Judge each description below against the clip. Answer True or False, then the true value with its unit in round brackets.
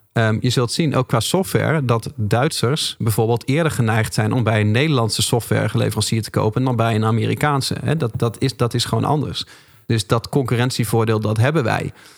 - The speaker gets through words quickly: False (185 wpm)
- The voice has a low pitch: True (120 Hz)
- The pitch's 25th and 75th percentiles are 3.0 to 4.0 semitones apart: True (3.7 semitones)